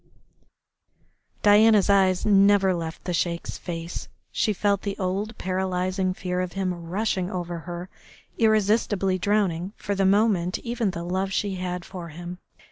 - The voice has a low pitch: No, medium, 185 Hz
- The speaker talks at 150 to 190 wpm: No, average, 140 wpm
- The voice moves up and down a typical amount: No, narrow, 2.3 semitones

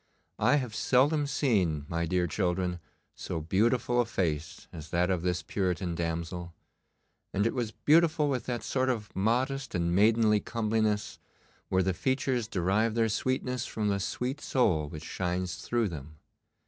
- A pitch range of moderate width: No, wide, 5.9 semitones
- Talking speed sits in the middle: Yes, average, 155 wpm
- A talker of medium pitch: No, low, 105 Hz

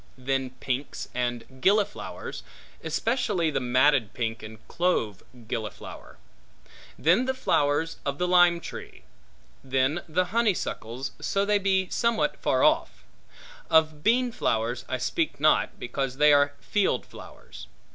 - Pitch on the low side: No, medium, 145 Hz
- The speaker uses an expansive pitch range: Yes, wide, 6.4 semitones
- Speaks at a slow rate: Yes, slow, 125 wpm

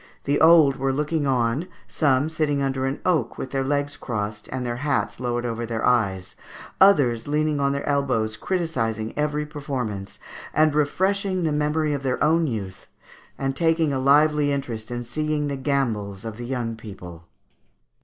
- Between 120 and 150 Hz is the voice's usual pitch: Yes, medium, 140 Hz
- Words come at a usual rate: Yes, average, 165 wpm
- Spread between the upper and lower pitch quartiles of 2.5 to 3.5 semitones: No, average, 4.2 semitones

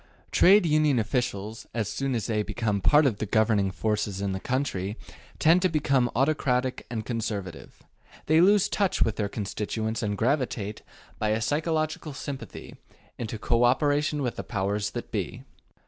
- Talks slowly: No, average, 160 wpm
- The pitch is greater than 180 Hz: No, low, 115 Hz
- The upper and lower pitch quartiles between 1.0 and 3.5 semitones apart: No, wide, 5.5 semitones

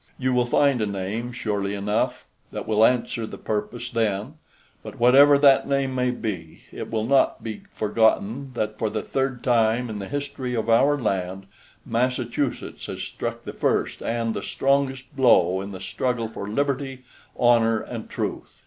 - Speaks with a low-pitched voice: Yes, low, 120 Hz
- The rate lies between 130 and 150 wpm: No, average, 165 wpm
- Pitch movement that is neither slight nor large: Yes, average, 3.5 semitones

